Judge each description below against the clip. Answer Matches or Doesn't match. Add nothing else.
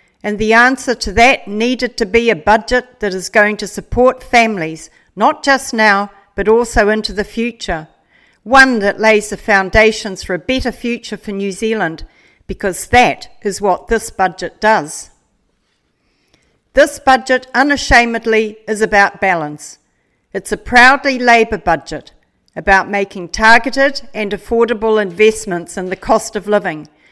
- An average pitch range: Matches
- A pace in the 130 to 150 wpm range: Matches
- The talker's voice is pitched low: Doesn't match